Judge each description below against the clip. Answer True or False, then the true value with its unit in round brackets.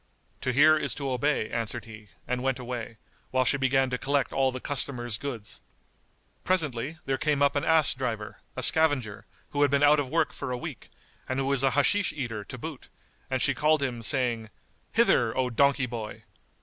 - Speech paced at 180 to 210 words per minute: True (195 wpm)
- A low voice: True (130 Hz)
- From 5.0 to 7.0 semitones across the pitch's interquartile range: False (3.0 semitones)